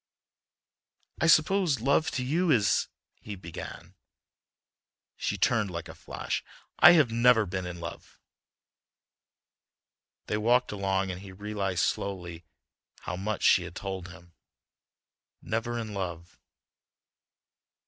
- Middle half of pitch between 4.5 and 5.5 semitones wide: Yes, average, 4.8 semitones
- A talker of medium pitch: No, low, 100 Hz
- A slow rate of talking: Yes, slow, 115 wpm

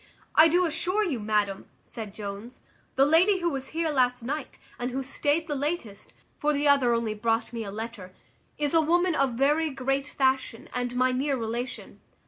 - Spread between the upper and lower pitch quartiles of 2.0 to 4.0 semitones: No, average, 4.6 semitones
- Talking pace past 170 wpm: Yes, average, 185 wpm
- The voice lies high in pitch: Yes, very high, 265 Hz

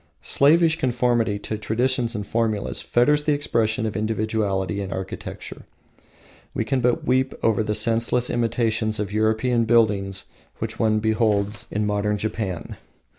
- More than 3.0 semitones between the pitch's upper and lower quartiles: No, narrow, 2.4 semitones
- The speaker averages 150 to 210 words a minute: No, slow, 135 wpm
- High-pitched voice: No, low, 110 Hz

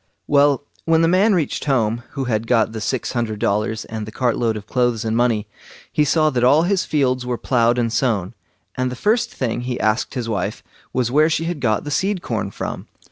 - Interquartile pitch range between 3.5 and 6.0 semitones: Yes, average, 4.6 semitones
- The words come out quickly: Yes, fast, 220 wpm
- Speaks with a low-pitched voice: Yes, low, 125 Hz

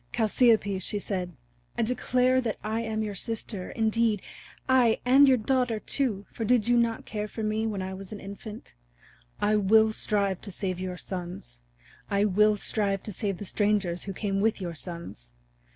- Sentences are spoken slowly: No, average, 180 wpm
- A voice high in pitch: Yes, high, 210 Hz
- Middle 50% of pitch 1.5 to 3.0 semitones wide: Yes, average, 2.7 semitones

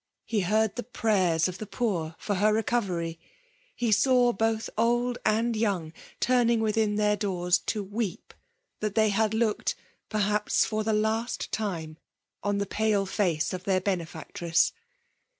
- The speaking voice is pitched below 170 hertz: No, high, 210 Hz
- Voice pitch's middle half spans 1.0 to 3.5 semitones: Yes, average, 3.0 semitones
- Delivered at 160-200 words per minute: No, average, 150 wpm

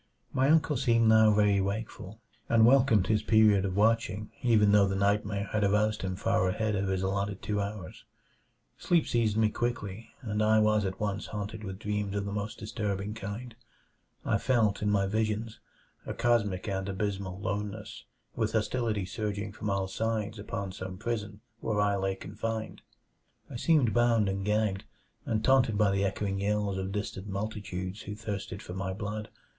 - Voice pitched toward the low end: Yes, low, 105 Hz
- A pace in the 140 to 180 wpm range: Yes, average, 170 wpm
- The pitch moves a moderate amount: No, narrow, 1.9 semitones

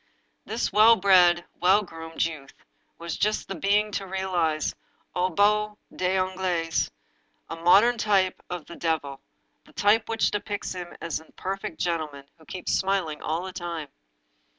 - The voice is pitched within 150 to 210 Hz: Yes, medium, 185 Hz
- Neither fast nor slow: Yes, average, 160 wpm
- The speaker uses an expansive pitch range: No, average, 3.4 semitones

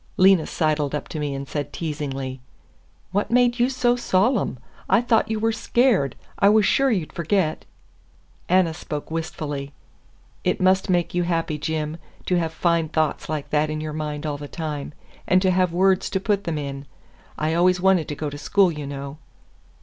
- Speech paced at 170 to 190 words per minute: Yes, average, 185 wpm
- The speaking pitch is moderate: Yes, medium, 165 Hz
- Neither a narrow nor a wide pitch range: Yes, average, 4.3 semitones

